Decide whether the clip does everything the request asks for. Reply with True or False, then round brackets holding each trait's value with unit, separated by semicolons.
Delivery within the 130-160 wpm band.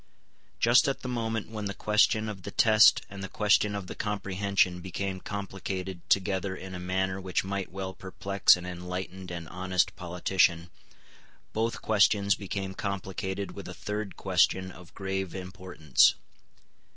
True (150 wpm)